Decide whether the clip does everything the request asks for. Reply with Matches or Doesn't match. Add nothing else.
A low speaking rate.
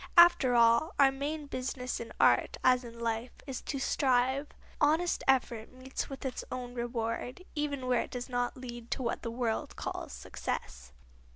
Doesn't match